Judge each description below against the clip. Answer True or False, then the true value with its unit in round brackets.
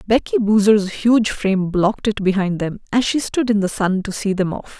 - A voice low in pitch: False (205 Hz)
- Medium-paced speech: False (225 wpm)